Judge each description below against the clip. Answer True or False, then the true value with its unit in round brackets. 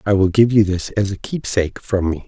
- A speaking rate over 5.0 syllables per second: True (5.6 syllables/s)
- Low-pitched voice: True (100 Hz)